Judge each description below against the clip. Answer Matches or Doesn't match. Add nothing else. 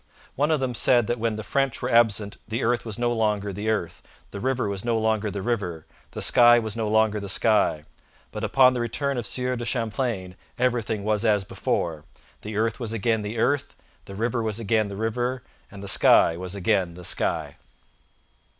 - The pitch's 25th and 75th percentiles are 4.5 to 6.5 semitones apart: Doesn't match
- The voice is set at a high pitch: Doesn't match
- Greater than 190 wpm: Matches